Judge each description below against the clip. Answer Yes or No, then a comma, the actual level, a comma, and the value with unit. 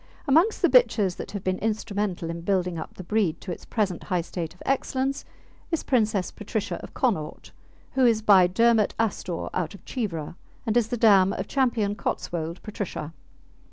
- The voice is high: Yes, high, 200 Hz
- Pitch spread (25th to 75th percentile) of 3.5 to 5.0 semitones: Yes, average, 4.3 semitones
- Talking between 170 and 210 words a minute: Yes, average, 175 wpm